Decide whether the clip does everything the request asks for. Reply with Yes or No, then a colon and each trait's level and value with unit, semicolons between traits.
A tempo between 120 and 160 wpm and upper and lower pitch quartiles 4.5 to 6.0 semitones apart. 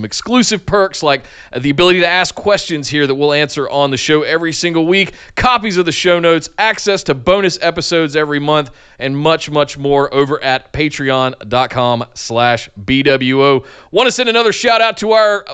No: average, 180 wpm; average, 4.8 semitones